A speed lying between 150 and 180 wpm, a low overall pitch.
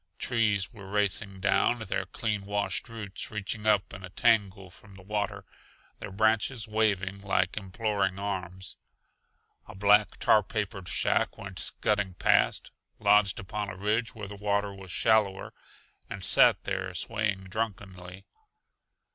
No: average, 140 wpm; low, 100 Hz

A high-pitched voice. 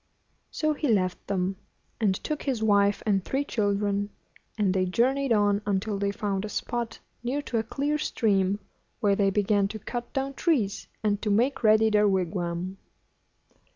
Yes: high, 210 Hz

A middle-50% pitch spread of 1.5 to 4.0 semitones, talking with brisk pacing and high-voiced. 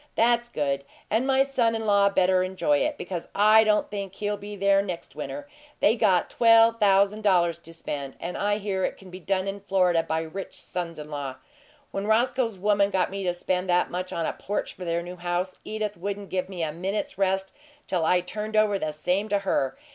Yes: average, 2.9 semitones; fast, 215 wpm; high, 195 Hz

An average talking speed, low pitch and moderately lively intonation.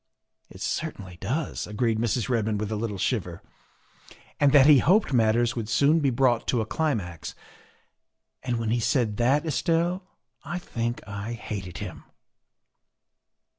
Yes: average, 150 wpm; low, 120 Hz; average, 4.6 semitones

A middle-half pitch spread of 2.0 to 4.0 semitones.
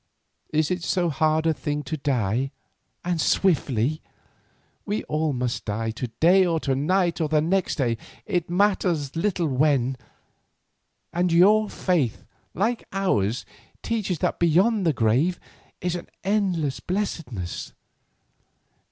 No: average, 5.3 semitones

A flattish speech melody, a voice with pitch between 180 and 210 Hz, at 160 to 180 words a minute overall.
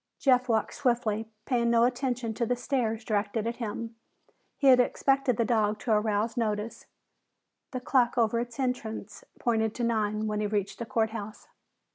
No: narrow, 2.3 semitones; high, 230 Hz; average, 170 wpm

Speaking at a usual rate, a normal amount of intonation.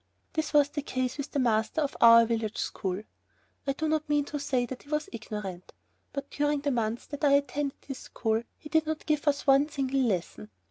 No: fast, 215 wpm; average, 4.2 semitones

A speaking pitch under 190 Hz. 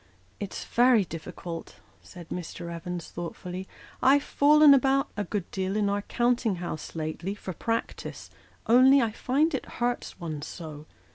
No: high, 200 Hz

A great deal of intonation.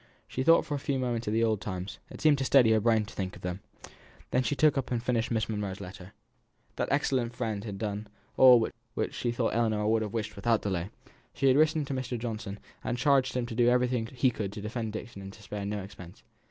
No: average, 3.4 semitones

